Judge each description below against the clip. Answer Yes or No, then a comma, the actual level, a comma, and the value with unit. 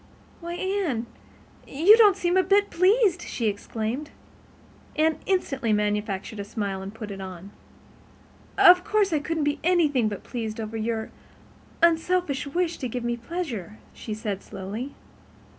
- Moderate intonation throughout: No, wide, 8.5 semitones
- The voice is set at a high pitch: Yes, very high, 265 Hz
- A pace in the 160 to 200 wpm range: No, average, 145 wpm